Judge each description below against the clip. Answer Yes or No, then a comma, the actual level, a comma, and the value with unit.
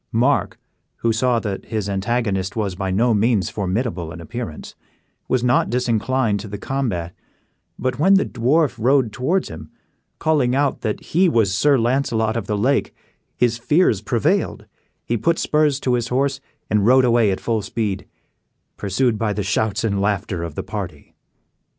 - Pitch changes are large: No, average, 4.1 semitones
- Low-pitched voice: Yes, low, 115 Hz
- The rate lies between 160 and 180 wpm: Yes, average, 165 wpm